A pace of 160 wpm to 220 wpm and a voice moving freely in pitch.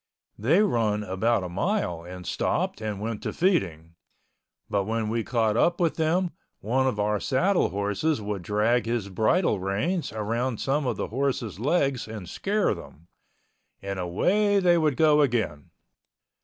No: average, 150 wpm; wide, 7.0 semitones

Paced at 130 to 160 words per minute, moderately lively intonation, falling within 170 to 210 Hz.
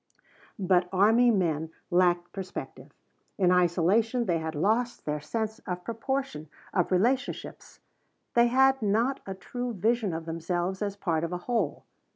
Yes: average, 145 wpm; average, 4.9 semitones; high, 190 Hz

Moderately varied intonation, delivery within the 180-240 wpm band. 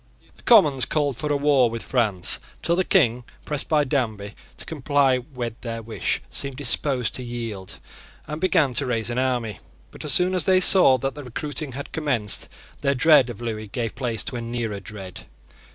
Yes: average, 4.1 semitones; average, 190 wpm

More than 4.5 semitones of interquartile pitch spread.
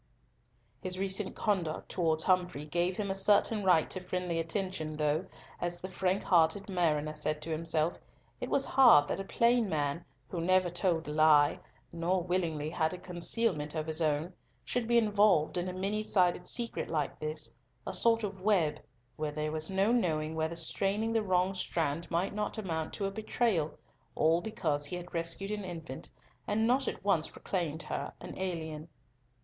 No: average, 3.8 semitones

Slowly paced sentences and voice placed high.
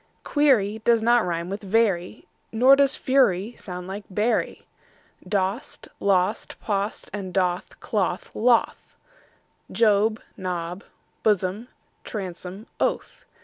Yes: slow, 105 wpm; high, 205 Hz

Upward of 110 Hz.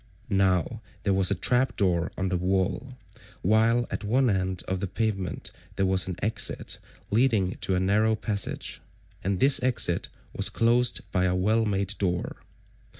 No: low, 100 Hz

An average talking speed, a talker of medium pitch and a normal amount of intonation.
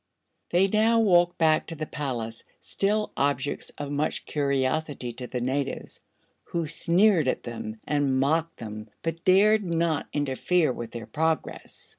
Yes: average, 145 wpm; medium, 150 Hz; average, 4.7 semitones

